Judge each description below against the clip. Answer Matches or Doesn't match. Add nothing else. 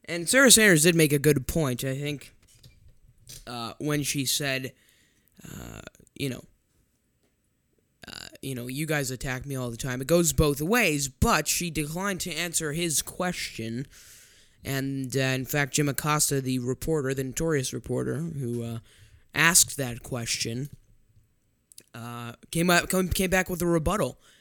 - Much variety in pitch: Doesn't match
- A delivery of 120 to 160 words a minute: Matches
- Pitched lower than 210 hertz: Matches